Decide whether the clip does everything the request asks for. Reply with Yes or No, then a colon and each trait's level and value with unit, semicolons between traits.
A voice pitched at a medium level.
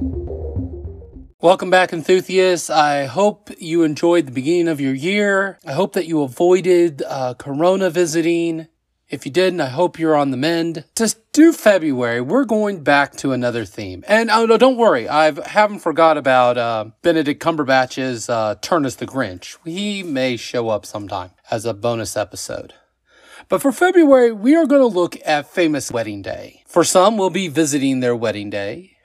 Yes: medium, 160 Hz